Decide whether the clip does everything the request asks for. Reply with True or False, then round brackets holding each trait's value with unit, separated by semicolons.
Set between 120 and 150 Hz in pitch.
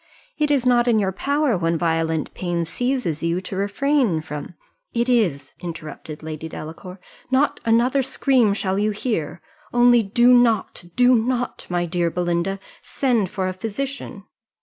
False (200 Hz)